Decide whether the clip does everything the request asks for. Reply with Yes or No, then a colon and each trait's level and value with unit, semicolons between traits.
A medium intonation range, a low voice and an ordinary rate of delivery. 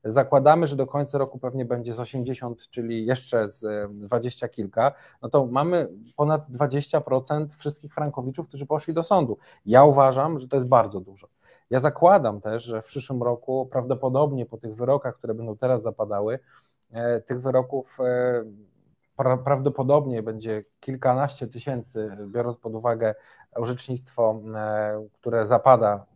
Yes: average, 3.6 semitones; low, 125 Hz; average, 135 wpm